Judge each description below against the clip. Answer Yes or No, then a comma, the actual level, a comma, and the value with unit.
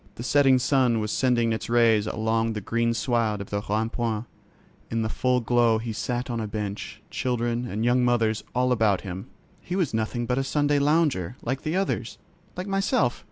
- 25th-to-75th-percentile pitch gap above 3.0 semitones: No, narrow, 2.4 semitones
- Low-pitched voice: Yes, low, 120 Hz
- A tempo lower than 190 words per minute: No, average, 195 wpm